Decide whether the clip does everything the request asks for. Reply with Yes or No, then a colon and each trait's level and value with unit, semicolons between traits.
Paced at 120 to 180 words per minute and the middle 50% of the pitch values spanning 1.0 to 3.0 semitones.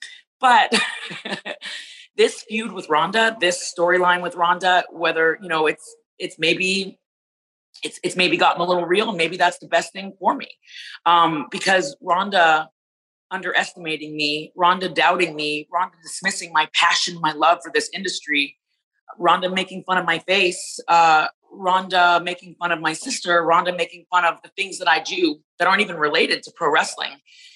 Yes: average, 165 wpm; narrow, 2.4 semitones